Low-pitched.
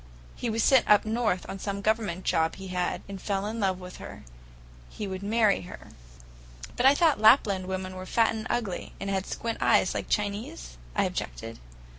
No: high, 200 Hz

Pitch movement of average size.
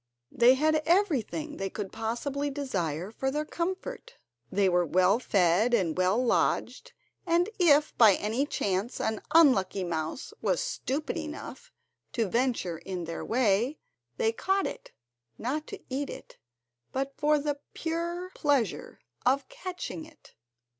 No: wide, 7.6 semitones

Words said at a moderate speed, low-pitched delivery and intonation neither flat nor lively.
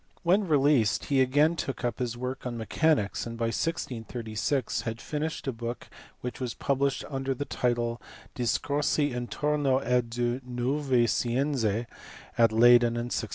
Yes: average, 150 wpm; low, 125 Hz; average, 3.1 semitones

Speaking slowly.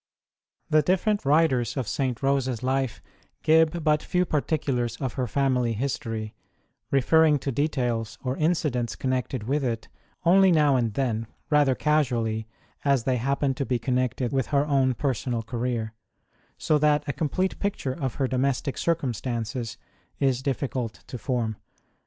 No: average, 145 wpm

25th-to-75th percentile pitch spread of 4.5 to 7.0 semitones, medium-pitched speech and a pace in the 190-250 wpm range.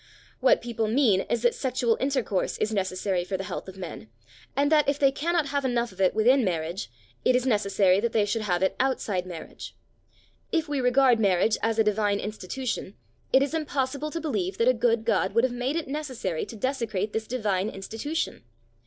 No: average, 5.1 semitones; high, 230 Hz; average, 195 wpm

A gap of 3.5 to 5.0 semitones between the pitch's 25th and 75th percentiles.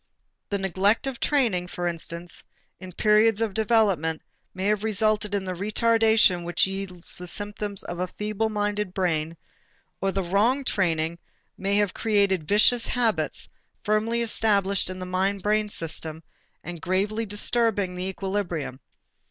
No: average, 2.9 semitones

